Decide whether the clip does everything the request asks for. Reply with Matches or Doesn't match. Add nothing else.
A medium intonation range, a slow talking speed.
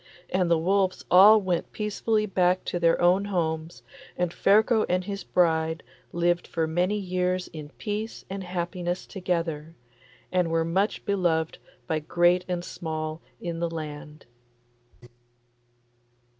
Doesn't match